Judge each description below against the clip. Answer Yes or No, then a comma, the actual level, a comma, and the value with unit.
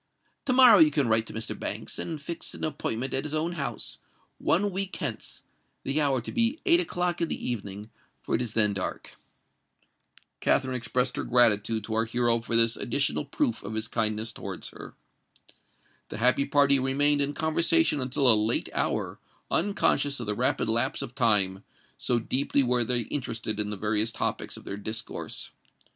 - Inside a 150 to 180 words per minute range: Yes, average, 175 wpm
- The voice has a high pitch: No, low, 125 Hz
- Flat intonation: No, average, 4.7 semitones